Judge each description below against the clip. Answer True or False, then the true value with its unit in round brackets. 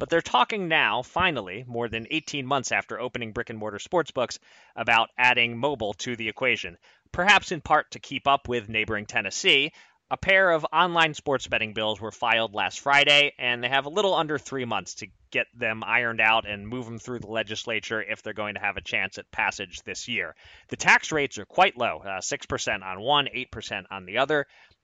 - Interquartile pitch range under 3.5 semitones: False (4.5 semitones)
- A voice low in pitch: True (120 Hz)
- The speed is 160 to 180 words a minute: False (205 wpm)